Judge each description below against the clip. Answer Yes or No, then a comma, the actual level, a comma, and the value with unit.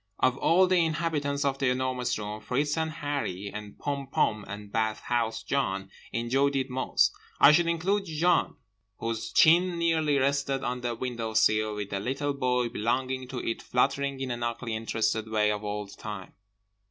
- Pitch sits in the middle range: No, low, 130 Hz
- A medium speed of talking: Yes, average, 170 wpm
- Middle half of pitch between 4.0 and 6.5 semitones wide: Yes, average, 4.4 semitones